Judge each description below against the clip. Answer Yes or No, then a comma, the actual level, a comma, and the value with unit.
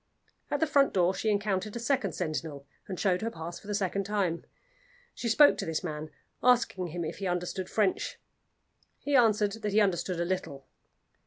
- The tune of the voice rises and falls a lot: No, average, 3.8 semitones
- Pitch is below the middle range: No, high, 195 Hz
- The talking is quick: No, average, 185 wpm